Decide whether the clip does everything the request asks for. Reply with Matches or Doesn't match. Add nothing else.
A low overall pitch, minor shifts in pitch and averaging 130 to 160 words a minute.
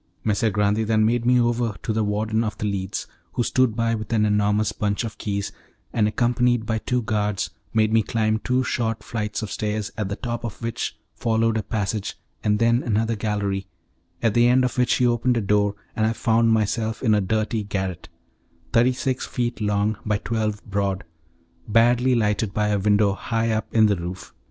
Doesn't match